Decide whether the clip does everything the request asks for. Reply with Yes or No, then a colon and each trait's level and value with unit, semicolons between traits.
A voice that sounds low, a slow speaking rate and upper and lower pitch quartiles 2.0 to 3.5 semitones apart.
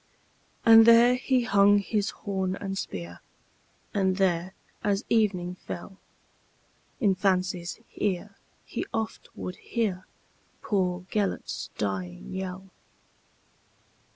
No: high, 195 Hz; slow, 90 wpm; narrow, 2.5 semitones